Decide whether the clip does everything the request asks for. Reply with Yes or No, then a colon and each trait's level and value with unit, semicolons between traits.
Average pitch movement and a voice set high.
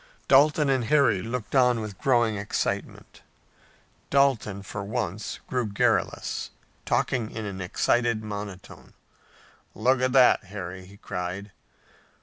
No: average, 4.2 semitones; low, 110 Hz